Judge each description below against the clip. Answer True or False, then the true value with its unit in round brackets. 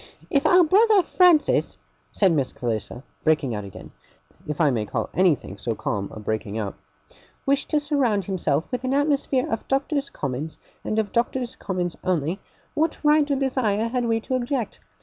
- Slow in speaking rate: False (170 wpm)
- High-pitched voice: True (220 Hz)